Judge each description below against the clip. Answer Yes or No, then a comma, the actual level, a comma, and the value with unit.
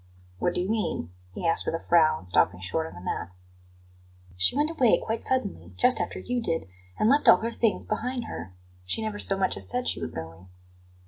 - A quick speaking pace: Yes, fast, 210 wpm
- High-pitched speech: Yes, high, 195 Hz